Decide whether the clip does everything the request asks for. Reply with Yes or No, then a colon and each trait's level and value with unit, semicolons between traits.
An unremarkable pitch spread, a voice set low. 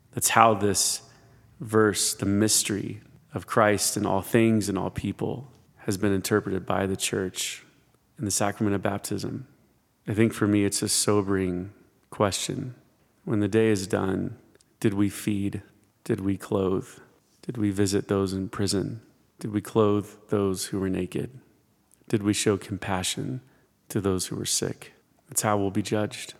No: narrow, 2.1 semitones; low, 105 Hz